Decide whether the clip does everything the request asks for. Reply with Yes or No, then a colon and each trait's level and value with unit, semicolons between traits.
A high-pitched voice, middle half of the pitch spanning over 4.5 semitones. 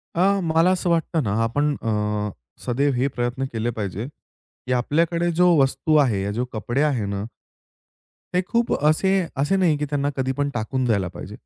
No: medium, 140 Hz; average, 5.1 semitones